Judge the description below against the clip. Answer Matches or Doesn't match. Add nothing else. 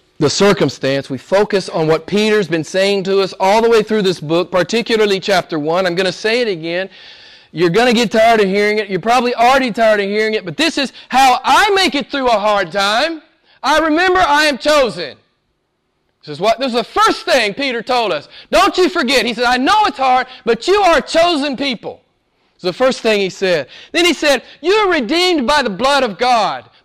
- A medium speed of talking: Doesn't match